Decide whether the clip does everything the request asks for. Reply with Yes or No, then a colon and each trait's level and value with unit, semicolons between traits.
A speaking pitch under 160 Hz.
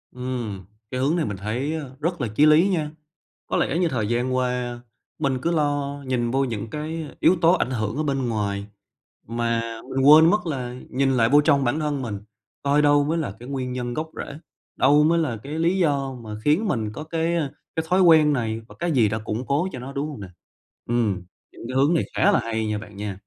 Yes: low, 135 Hz